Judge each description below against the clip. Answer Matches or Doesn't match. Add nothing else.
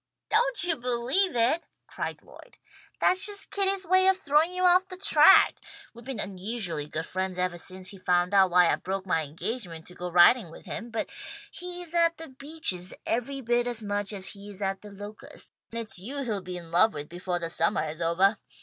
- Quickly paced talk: Matches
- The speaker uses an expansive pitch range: Matches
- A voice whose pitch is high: Matches